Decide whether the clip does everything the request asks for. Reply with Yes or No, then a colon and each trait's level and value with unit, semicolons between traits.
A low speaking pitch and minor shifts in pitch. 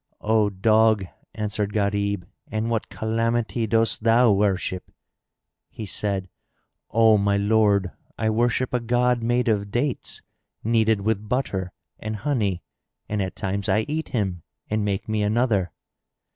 Yes: low, 110 Hz; narrow, 2.2 semitones